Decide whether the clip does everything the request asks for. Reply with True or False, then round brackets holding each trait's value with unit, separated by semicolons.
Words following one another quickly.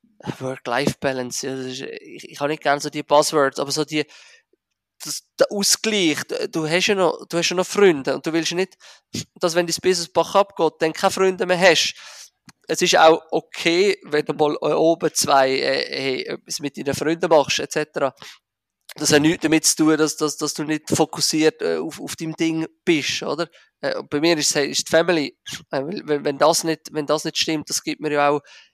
True (195 wpm)